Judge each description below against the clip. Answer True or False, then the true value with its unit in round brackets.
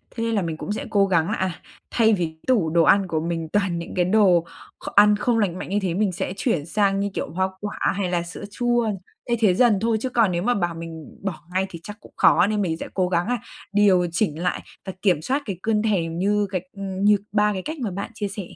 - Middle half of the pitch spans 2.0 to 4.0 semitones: True (3.3 semitones)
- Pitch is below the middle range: False (195 Hz)